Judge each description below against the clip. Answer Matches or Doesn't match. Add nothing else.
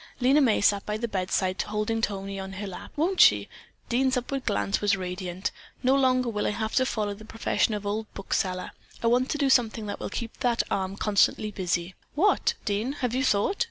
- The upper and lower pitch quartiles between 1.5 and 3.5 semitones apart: Doesn't match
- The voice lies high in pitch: Matches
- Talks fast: Matches